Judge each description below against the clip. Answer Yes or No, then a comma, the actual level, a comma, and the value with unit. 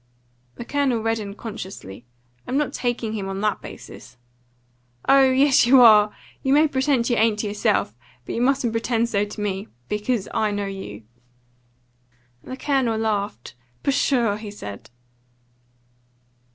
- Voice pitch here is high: Yes, high, 225 Hz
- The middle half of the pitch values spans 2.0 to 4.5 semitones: Yes, average, 4.0 semitones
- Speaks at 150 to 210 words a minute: No, average, 140 wpm